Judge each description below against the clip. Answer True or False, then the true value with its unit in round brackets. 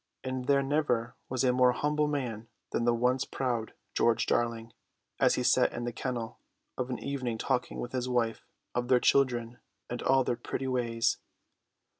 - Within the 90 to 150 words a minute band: False (175 wpm)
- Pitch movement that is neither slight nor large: False (1.9 semitones)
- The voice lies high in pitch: False (125 Hz)